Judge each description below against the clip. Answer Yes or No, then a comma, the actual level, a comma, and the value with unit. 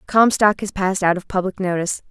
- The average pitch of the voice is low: No, high, 190 Hz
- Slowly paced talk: No, average, 200 wpm